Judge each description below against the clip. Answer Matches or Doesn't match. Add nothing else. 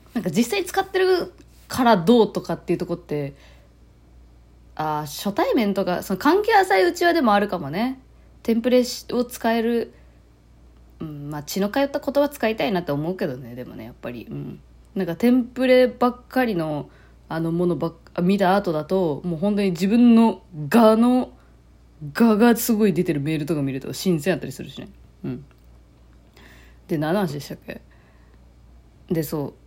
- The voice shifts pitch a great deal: Matches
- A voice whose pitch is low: Doesn't match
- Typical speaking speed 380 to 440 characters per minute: Doesn't match